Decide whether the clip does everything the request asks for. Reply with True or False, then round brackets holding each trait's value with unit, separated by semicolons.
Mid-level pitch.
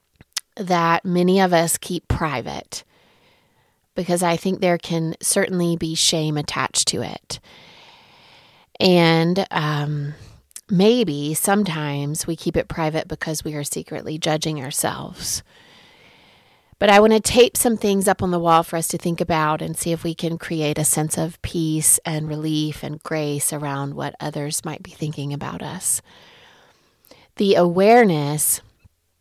True (165 Hz)